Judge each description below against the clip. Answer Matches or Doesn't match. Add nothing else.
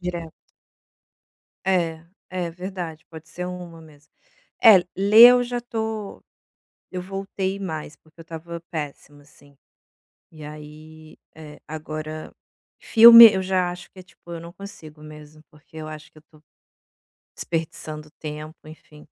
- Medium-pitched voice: Matches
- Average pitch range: Matches